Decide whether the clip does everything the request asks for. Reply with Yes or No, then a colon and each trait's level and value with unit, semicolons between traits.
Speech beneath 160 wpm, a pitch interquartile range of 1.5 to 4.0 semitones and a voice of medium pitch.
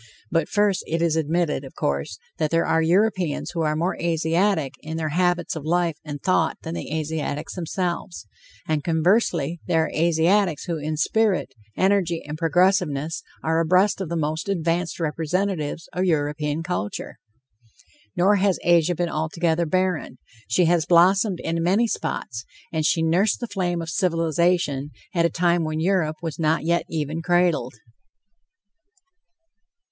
Yes: average, 150 wpm; narrow, 2.4 semitones; medium, 165 Hz